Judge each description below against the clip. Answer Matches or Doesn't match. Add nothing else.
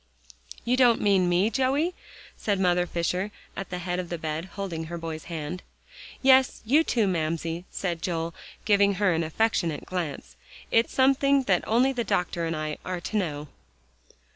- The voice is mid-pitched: Matches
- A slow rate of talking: Doesn't match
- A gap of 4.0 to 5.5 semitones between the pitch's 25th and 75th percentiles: Matches